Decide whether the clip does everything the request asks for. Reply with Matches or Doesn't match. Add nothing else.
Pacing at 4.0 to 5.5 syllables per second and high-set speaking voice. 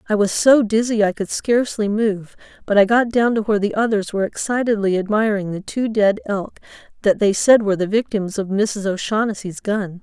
Matches